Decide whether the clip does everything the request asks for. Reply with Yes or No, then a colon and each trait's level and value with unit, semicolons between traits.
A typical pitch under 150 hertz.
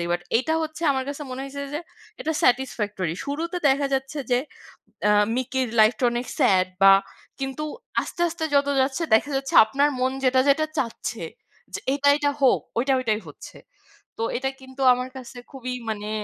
No: very high, 265 Hz